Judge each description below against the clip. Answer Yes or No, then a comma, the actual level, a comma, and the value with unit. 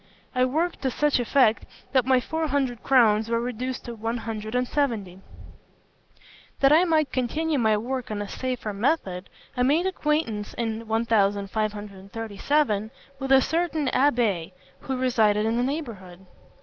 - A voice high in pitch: Yes, high, 240 Hz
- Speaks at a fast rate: No, average, 150 wpm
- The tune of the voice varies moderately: Yes, average, 4.2 semitones